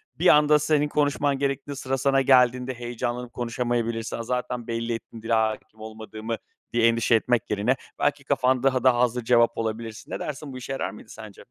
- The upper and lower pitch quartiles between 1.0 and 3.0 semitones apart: Yes, average, 2.7 semitones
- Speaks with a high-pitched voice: No, low, 120 Hz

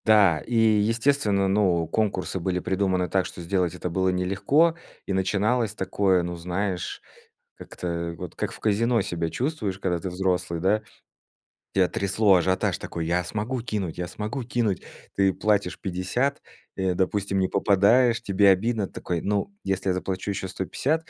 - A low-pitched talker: Yes, very low, 95 Hz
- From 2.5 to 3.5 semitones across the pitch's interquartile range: Yes, average, 2.9 semitones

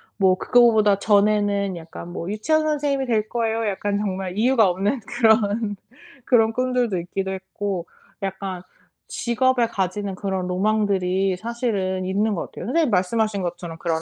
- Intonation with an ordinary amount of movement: Yes, average, 3.3 semitones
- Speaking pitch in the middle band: No, high, 205 Hz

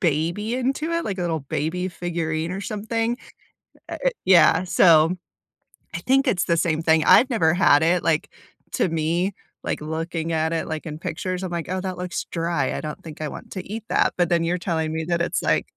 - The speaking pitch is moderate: Yes, medium, 170 Hz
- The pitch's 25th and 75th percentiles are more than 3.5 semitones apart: No, average, 2.8 semitones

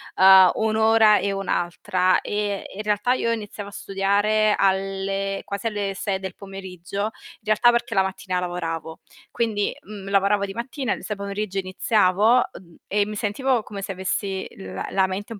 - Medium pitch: No, high, 200 Hz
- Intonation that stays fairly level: Yes, narrow, 1.9 semitones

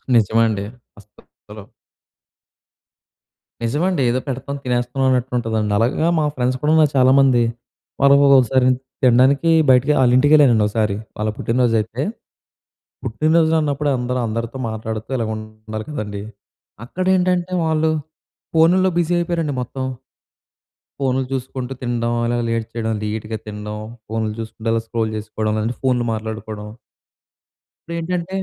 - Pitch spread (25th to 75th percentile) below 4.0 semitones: No, average, 4.3 semitones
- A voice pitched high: No, low, 125 Hz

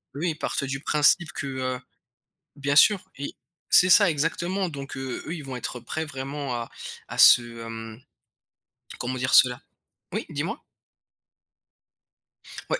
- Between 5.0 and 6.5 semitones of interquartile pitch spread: No, average, 3.5 semitones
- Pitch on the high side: No, medium, 140 Hz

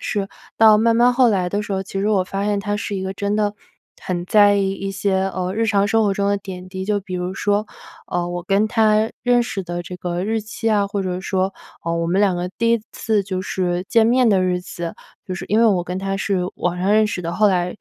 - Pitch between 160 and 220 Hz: Yes, high, 195 Hz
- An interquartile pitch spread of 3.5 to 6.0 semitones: No, narrow, 2.5 semitones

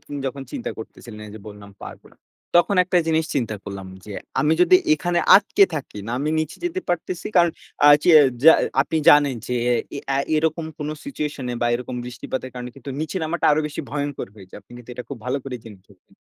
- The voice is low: No, medium, 145 Hz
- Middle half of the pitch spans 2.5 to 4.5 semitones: No, average, 5.0 semitones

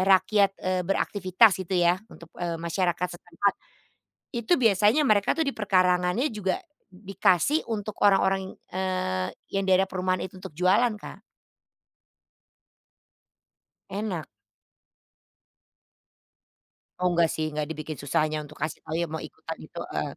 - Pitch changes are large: No, average, 2.8 semitones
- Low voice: No, medium, 185 Hz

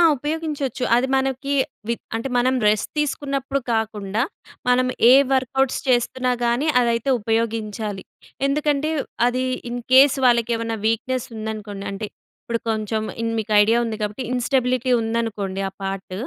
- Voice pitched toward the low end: No, high, 235 Hz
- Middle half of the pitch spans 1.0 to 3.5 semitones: Yes, average, 3.1 semitones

